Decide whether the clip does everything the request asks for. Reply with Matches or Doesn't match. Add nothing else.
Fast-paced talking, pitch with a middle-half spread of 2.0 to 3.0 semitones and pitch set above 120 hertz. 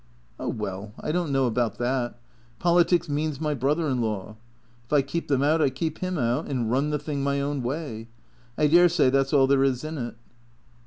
Doesn't match